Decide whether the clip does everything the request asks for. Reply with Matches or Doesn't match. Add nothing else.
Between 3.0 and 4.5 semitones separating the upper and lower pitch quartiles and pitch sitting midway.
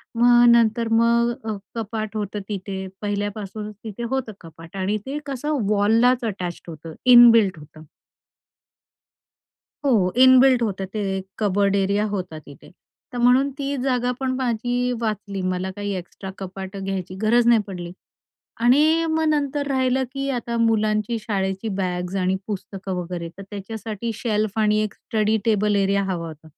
Doesn't match